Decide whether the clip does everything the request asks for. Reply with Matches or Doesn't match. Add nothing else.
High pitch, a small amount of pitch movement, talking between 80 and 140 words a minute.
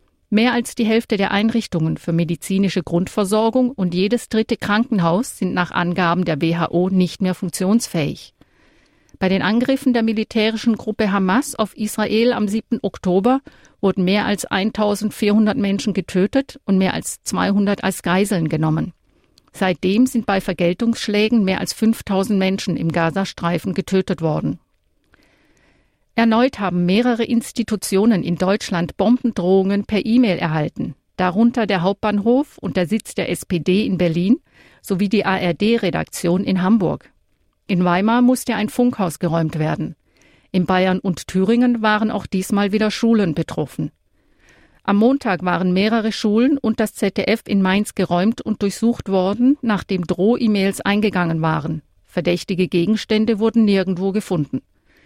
Doesn't match